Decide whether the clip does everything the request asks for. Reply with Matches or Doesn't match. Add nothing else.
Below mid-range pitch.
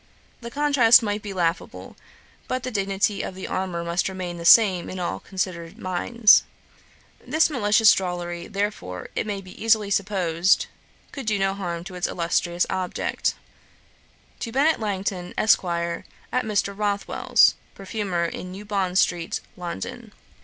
Doesn't match